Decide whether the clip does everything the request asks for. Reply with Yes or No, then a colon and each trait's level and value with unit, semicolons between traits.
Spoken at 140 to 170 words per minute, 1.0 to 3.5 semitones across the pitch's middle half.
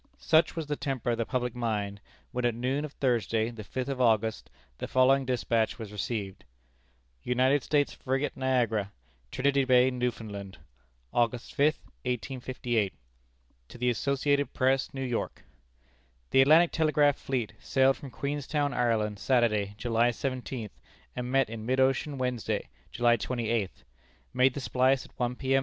Yes: average, 150 wpm; average, 2.8 semitones